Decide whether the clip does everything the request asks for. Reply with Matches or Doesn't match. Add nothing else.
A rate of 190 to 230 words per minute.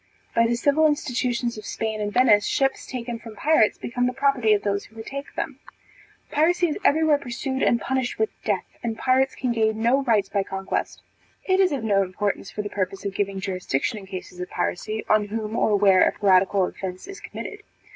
Matches